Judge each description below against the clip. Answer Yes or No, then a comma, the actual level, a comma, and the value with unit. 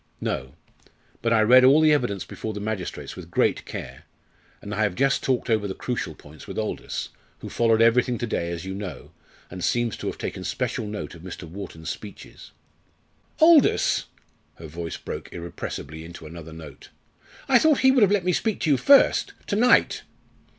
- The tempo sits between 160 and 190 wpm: Yes, average, 185 wpm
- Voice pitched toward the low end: Yes, low, 110 Hz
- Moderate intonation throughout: No, wide, 7.6 semitones